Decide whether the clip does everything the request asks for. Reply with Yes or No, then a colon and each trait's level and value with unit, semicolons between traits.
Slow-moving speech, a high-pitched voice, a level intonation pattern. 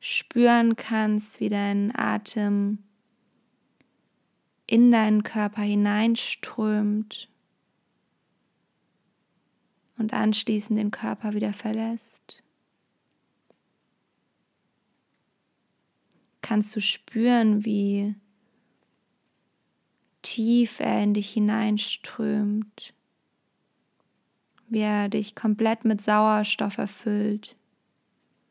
Yes: slow, 65 wpm; high, 215 Hz; narrow, 1.4 semitones